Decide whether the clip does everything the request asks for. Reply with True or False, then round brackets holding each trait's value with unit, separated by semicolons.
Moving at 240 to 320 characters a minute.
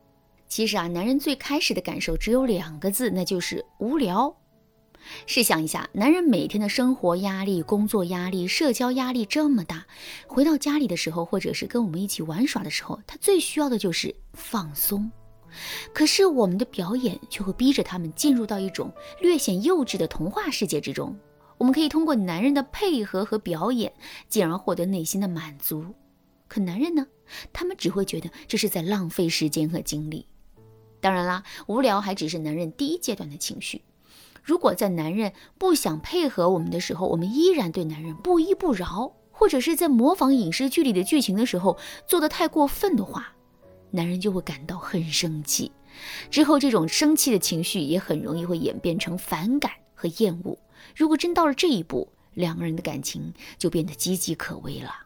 True (290 characters per minute)